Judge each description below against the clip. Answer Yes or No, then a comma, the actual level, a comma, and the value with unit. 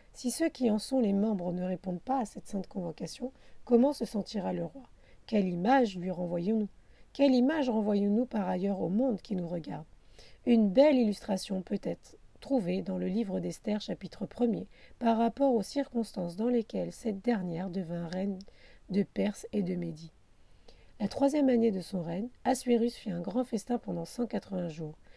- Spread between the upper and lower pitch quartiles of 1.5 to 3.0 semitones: No, average, 4.8 semitones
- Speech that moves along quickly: No, average, 175 wpm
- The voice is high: Yes, high, 205 Hz